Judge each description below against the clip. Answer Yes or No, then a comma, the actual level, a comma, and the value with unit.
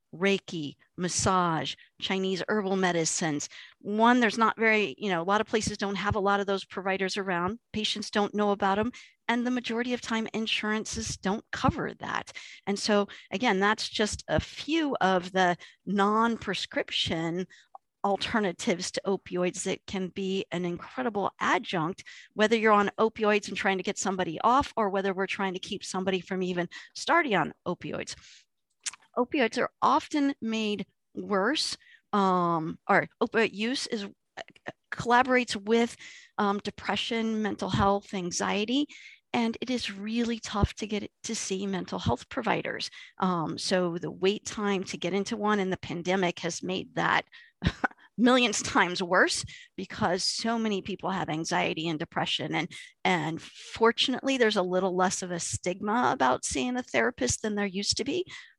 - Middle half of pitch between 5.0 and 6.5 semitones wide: No, average, 3.4 semitones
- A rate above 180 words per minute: No, average, 160 wpm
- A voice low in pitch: No, high, 200 Hz